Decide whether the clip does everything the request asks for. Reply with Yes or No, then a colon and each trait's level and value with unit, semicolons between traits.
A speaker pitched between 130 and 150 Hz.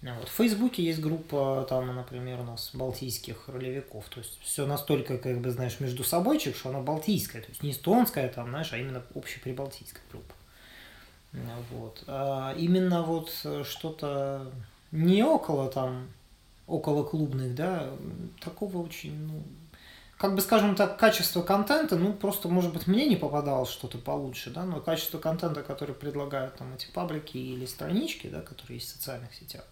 Yes: medium, 140 Hz